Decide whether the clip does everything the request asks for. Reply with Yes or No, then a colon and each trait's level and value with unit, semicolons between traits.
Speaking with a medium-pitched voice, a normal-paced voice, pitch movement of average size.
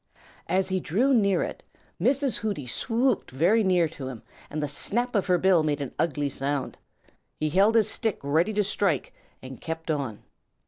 No: medium, 175 Hz; average, 180 wpm; wide, 6.5 semitones